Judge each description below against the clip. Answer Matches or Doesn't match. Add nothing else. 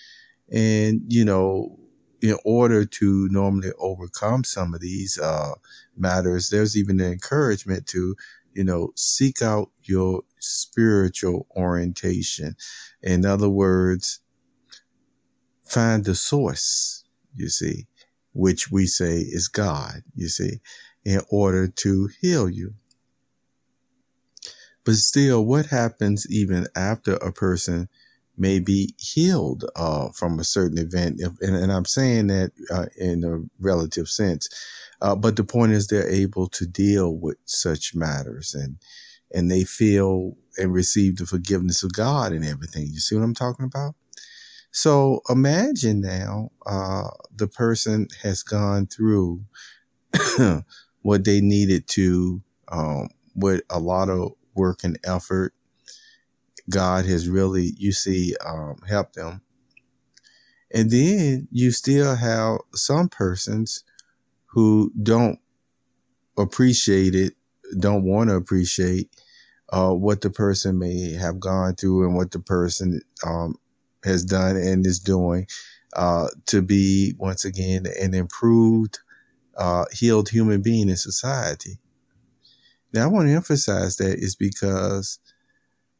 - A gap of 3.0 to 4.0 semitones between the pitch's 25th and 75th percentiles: Matches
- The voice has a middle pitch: Doesn't match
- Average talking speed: Doesn't match